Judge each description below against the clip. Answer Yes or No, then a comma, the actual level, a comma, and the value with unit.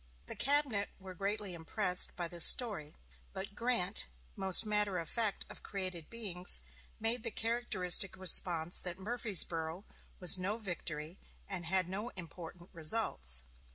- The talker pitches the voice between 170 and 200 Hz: Yes, high, 190 Hz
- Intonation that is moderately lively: Yes, average, 3.6 semitones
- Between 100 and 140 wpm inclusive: Yes, slow, 135 wpm